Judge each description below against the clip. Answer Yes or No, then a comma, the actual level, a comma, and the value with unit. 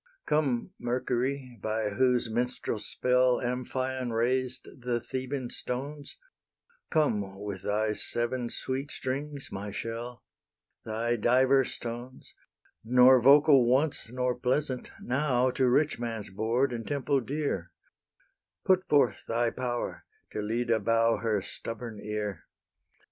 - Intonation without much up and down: Yes, narrow, 2.3 semitones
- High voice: No, low, 125 Hz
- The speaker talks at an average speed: No, slow, 115 wpm